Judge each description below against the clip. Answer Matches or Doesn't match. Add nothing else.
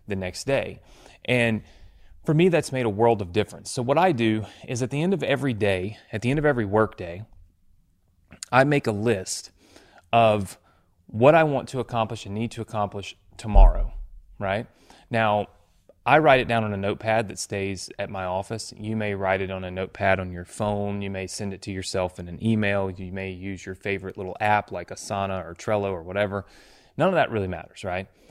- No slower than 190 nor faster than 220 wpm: Matches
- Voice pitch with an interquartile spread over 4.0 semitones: Doesn't match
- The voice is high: Doesn't match